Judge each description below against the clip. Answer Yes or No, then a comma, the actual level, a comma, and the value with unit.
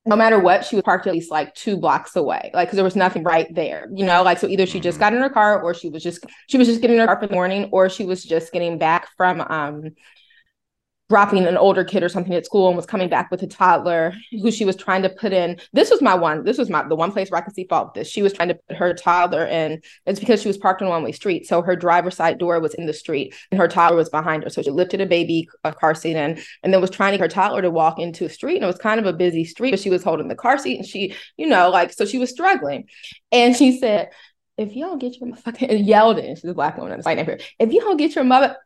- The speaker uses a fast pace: Yes, fast, 300 wpm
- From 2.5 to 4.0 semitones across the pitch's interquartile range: Yes, average, 3.7 semitones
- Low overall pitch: No, medium, 185 Hz